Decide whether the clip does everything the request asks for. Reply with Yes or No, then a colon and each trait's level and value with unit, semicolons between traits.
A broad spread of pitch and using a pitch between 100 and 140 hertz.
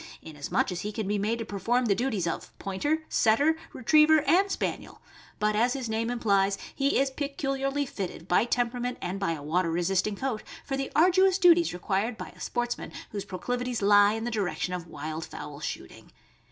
No: wide, 5.9 semitones; high, 225 Hz